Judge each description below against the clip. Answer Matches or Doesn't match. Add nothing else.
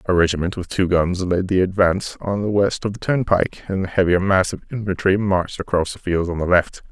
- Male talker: Matches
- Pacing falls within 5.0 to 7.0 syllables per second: Matches